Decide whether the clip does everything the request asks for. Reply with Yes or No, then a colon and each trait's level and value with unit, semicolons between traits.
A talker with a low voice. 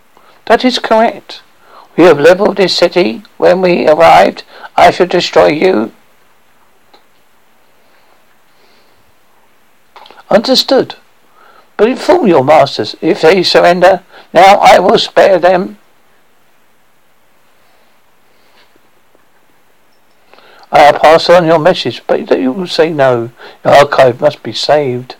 No: medium, 180 Hz